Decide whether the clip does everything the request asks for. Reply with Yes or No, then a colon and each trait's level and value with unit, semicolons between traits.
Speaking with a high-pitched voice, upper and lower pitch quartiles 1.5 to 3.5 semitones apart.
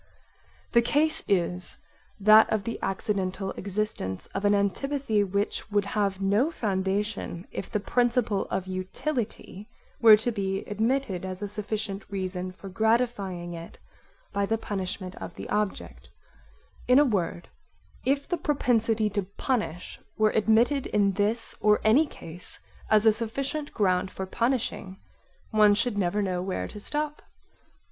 Yes: high, 210 Hz; average, 3.2 semitones